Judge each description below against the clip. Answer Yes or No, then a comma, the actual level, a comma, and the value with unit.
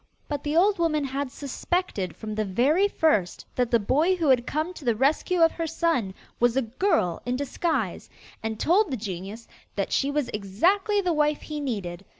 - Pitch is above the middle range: Yes, very high, 280 Hz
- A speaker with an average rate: Yes, average, 190 wpm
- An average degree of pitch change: No, wide, 6.9 semitones